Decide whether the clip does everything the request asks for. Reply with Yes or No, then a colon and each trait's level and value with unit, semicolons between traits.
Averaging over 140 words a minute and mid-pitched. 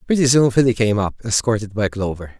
No: average, 200 wpm; low, 110 Hz